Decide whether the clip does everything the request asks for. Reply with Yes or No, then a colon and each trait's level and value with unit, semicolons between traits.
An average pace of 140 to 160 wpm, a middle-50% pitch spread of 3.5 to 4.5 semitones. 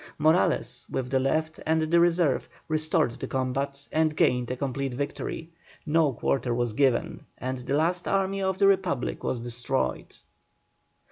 Yes: average, 150 wpm; average, 4.1 semitones